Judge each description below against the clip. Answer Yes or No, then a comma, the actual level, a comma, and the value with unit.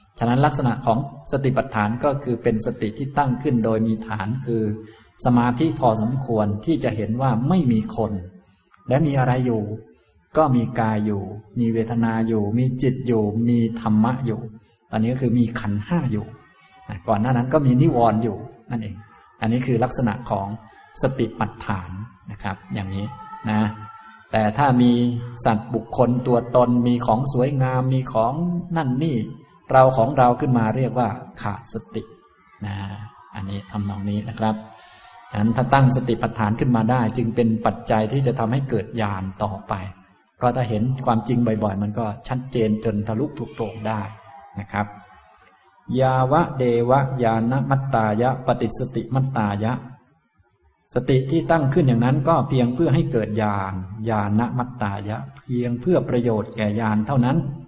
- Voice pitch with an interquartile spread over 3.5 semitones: No, average, 2.8 semitones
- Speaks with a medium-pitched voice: No, low, 115 Hz